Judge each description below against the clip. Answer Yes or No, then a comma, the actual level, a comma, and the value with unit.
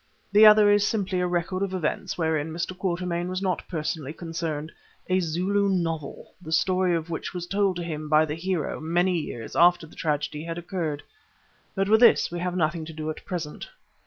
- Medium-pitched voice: Yes, medium, 175 Hz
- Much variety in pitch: No, average, 2.7 semitones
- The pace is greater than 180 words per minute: Yes, average, 190 wpm